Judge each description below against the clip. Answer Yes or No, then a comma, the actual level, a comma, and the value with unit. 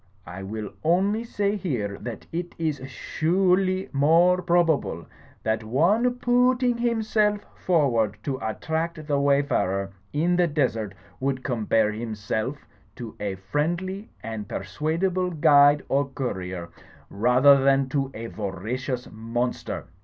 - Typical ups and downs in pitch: No, wide, 8.0 semitones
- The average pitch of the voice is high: No, medium, 140 Hz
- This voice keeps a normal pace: No, slow, 125 wpm